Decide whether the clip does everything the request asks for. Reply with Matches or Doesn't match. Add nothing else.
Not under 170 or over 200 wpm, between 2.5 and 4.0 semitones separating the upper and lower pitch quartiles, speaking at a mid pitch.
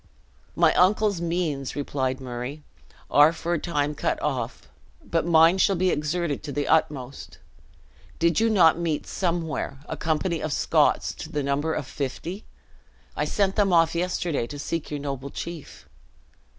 Doesn't match